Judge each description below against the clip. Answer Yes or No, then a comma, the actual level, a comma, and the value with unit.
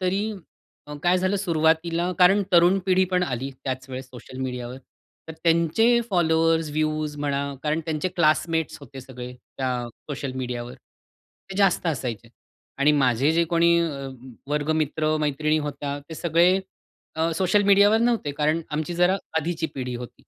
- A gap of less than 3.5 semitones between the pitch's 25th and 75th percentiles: No, average, 4.0 semitones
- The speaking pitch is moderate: Yes, medium, 160 Hz